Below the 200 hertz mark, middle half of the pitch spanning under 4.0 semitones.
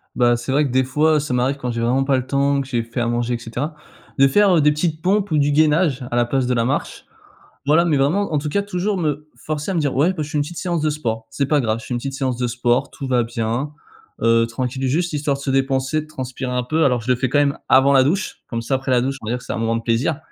Yes: low, 135 Hz; average, 3.6 semitones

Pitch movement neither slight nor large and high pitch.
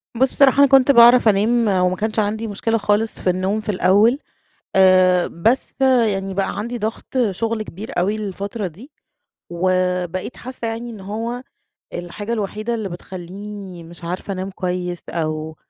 Yes: average, 3.7 semitones; high, 205 Hz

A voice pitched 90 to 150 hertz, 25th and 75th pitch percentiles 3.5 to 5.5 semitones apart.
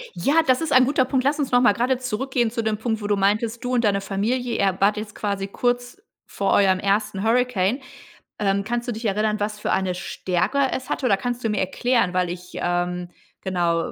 No: high, 215 Hz; average, 4.1 semitones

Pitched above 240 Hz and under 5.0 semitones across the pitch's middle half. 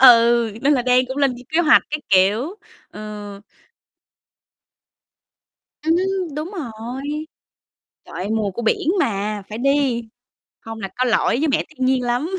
No: very high, 250 Hz; average, 5.3 semitones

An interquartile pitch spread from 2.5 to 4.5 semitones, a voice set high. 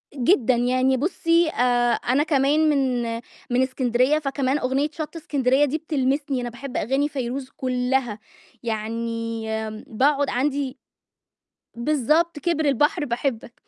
Yes: average, 3.3 semitones; very high, 265 Hz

